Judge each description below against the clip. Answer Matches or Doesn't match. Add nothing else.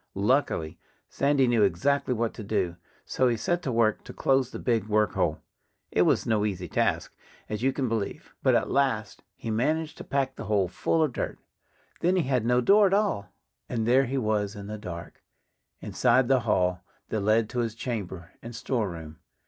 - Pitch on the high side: Doesn't match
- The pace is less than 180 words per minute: Doesn't match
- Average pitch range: Matches